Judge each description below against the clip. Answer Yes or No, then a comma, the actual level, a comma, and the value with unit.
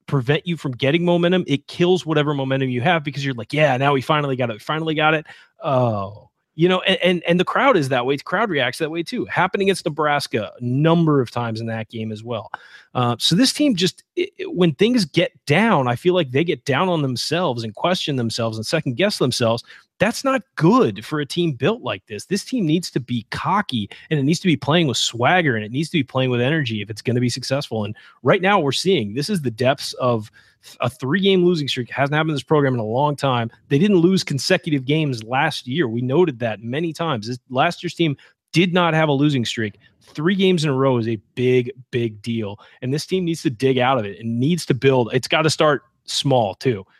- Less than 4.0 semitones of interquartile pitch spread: No, wide, 5.5 semitones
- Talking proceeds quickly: Yes, fast, 245 wpm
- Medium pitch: Yes, medium, 145 Hz